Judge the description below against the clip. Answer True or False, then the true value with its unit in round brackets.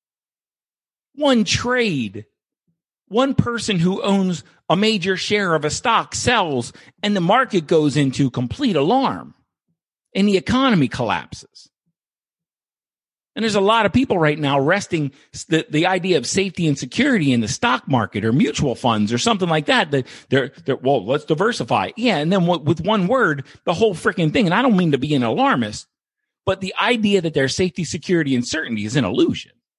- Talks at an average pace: True (175 wpm)